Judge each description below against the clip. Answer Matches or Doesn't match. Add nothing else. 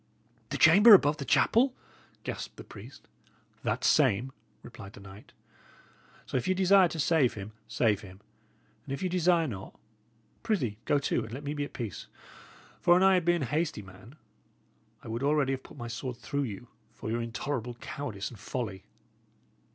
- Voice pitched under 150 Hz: Matches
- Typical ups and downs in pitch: Doesn't match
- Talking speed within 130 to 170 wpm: Doesn't match